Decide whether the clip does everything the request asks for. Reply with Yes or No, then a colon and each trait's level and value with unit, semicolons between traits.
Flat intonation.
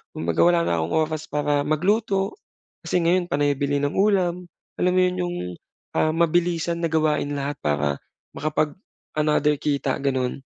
No: average, 3.6 semitones